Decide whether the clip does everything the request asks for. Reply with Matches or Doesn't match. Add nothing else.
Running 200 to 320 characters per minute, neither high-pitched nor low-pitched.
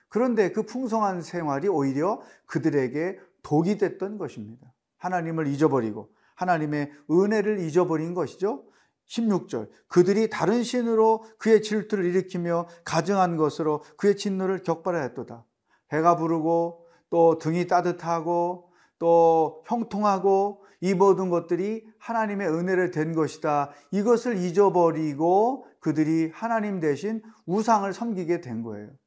Matches